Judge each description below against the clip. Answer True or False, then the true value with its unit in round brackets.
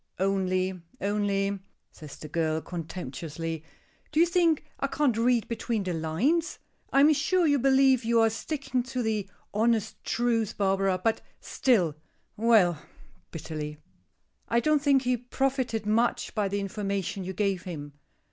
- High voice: True (215 Hz)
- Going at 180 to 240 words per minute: False (145 wpm)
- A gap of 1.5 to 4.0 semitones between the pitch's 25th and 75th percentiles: False (5.5 semitones)